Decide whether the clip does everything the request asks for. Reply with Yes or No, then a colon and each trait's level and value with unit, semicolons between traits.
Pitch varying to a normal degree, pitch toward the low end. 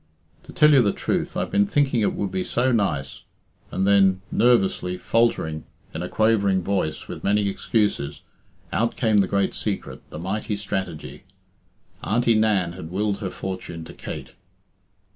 Yes: average, 3.0 semitones; low, 100 Hz